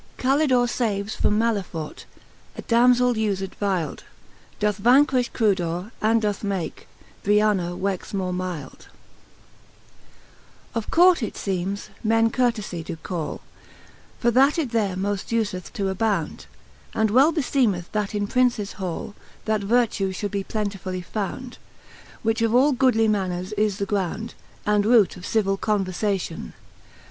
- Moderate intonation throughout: Yes, average, 3.3 semitones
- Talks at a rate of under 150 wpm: Yes, slow, 135 wpm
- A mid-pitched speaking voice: No, high, 210 Hz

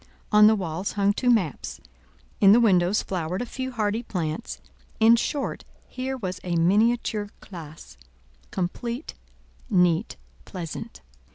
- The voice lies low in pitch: No, high, 200 Hz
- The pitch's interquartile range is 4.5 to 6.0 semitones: Yes, average, 5.1 semitones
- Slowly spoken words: Yes, slow, 120 wpm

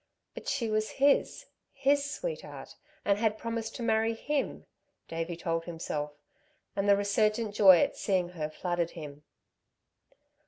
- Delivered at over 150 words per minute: No, average, 140 wpm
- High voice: Yes, high, 205 Hz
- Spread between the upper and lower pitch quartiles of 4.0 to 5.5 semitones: Yes, average, 5.0 semitones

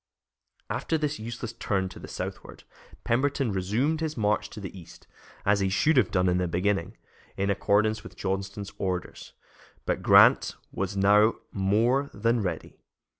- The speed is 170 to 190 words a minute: No, average, 155 wpm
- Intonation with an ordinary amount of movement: Yes, average, 3.4 semitones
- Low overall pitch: Yes, low, 105 Hz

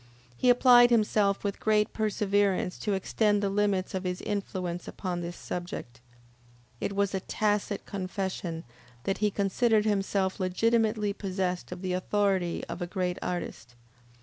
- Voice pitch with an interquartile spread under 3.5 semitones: Yes, narrow, 2.4 semitones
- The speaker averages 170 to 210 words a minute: No, average, 145 wpm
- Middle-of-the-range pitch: No, high, 195 Hz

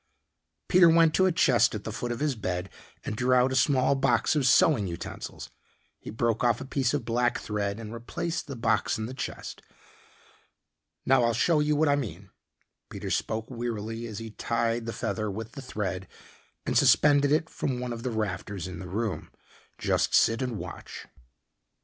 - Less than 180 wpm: No, average, 185 wpm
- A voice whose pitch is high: No, low, 120 Hz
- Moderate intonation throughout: Yes, average, 3.8 semitones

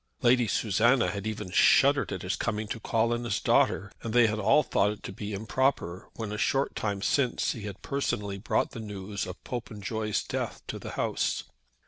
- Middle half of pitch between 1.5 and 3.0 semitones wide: Yes, average, 2.7 semitones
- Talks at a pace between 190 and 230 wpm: Yes, average, 195 wpm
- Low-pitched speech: Yes, low, 110 Hz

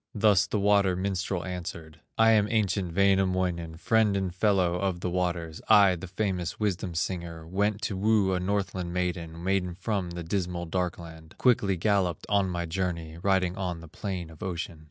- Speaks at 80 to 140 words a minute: No, average, 170 wpm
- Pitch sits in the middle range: No, very low, 90 Hz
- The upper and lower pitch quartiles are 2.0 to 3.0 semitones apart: Yes, narrow, 2.4 semitones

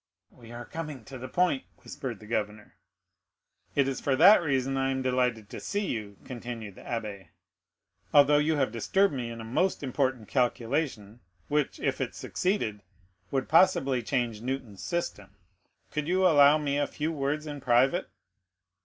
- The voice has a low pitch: Yes, low, 130 Hz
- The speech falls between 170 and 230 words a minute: No, average, 160 wpm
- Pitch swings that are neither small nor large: Yes, average, 4.2 semitones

